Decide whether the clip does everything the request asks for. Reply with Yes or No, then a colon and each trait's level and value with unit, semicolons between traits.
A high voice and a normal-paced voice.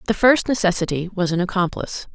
Yes: high, 195 Hz; average, 170 wpm